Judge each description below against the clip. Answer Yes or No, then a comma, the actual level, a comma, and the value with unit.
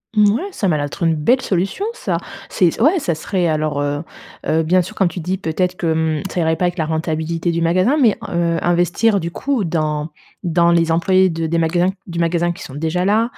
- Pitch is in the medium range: Yes, medium, 170 Hz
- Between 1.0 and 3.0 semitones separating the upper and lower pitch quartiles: Yes, narrow, 2.6 semitones